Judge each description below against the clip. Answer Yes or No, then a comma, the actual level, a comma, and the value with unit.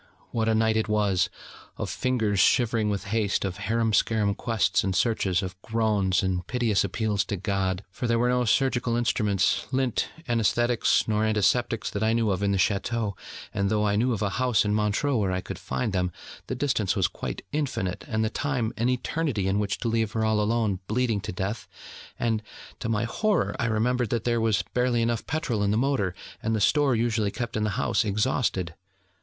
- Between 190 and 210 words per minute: Yes, average, 200 wpm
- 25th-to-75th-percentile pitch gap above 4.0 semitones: No, average, 2.9 semitones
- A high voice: No, low, 110 Hz